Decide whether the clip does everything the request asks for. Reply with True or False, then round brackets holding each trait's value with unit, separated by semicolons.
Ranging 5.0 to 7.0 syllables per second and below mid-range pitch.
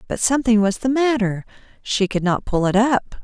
False (5.2 syllables/s; 225 Hz)